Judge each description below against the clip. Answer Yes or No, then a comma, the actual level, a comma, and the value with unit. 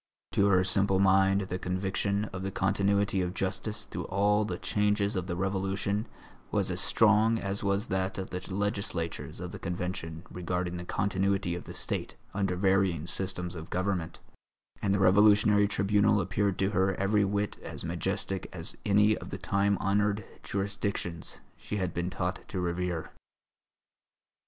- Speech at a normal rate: Yes, average, 160 wpm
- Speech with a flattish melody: Yes, narrow, 1.8 semitones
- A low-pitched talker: Yes, very low, 95 Hz